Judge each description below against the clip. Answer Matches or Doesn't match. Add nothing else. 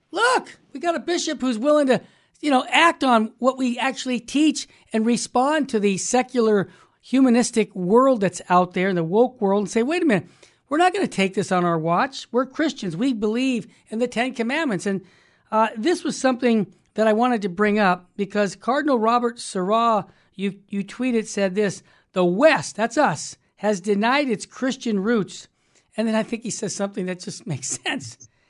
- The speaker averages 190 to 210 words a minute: Matches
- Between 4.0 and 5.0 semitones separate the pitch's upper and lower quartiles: Matches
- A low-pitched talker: Doesn't match